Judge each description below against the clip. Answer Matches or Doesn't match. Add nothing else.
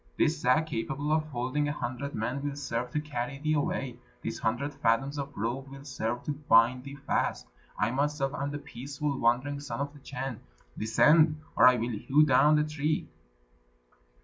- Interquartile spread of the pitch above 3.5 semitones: Doesn't match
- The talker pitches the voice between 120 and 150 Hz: Matches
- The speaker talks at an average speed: Matches